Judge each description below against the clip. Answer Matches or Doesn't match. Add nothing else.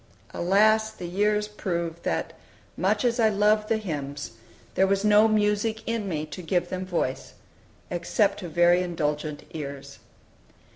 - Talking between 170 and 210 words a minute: Doesn't match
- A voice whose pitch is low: Doesn't match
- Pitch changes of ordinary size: Matches